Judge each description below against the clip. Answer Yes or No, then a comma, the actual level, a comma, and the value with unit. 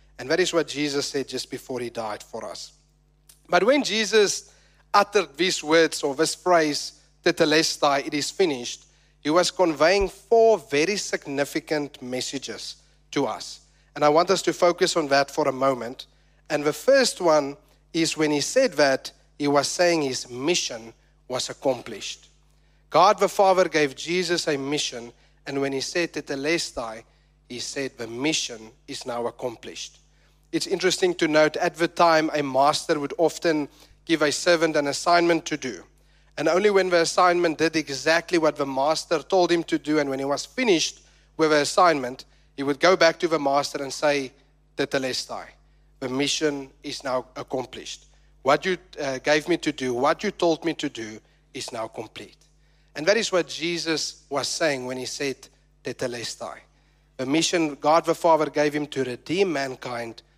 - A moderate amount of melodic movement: Yes, average, 3.5 semitones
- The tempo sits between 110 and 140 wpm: No, average, 170 wpm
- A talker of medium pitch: Yes, medium, 150 Hz